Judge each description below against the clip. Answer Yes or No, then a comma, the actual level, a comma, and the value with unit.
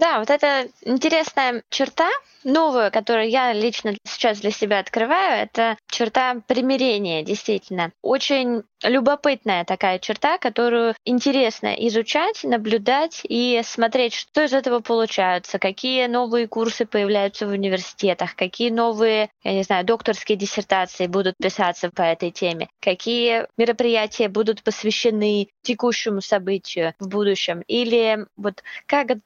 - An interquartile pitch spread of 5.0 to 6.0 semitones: No, average, 3.6 semitones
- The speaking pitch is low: No, high, 225 Hz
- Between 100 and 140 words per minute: Yes, average, 125 wpm